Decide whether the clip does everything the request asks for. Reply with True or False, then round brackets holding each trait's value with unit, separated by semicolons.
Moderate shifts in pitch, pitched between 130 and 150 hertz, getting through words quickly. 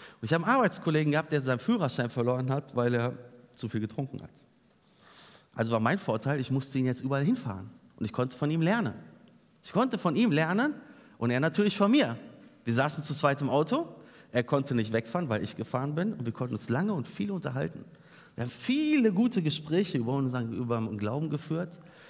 False (6.3 semitones; 140 Hz; 205 wpm)